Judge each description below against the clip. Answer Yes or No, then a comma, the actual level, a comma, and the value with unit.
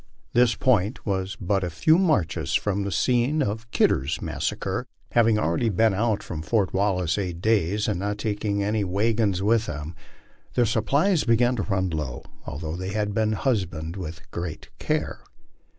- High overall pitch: No, low, 105 Hz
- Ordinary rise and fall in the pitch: Yes, average, 4.0 semitones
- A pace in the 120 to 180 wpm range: Yes, average, 160 wpm